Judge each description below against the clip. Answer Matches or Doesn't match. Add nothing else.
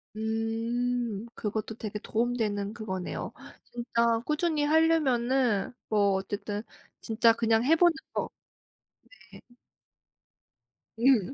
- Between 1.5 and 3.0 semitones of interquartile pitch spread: Matches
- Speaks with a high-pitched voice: Matches